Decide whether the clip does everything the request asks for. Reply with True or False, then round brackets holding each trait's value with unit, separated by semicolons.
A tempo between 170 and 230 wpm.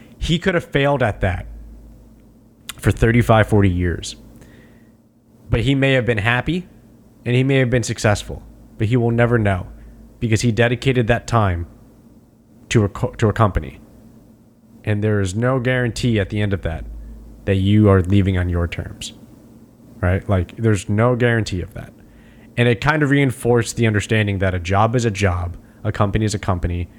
True (175 wpm)